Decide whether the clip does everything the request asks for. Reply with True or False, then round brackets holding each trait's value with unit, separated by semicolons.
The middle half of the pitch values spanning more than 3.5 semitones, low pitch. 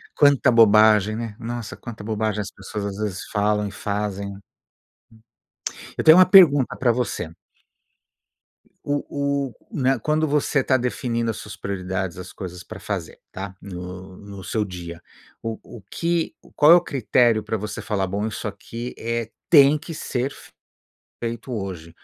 True (4.0 semitones; 110 Hz)